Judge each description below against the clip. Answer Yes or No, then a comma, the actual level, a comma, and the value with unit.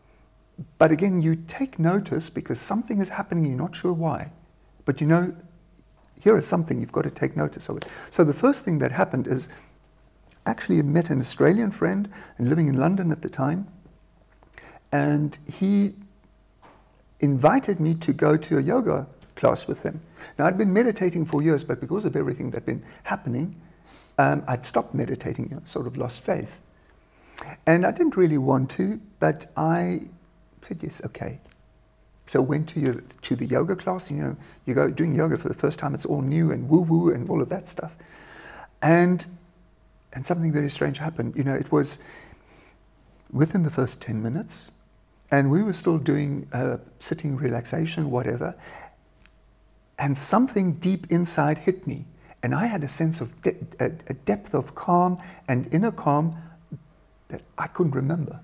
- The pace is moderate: No, fast, 175 wpm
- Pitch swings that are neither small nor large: Yes, average, 3.9 semitones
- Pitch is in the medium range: Yes, medium, 160 Hz